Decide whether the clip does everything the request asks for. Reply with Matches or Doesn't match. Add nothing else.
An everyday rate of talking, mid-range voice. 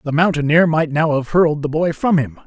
Doesn't match